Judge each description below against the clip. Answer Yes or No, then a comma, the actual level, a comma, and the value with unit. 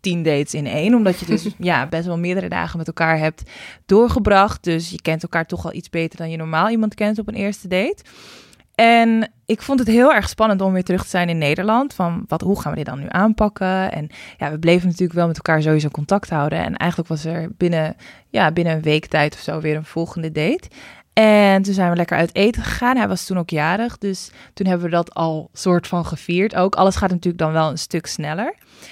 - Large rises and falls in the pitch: No, average, 3.6 semitones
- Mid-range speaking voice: Yes, medium, 175 Hz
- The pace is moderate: No, fast, 235 wpm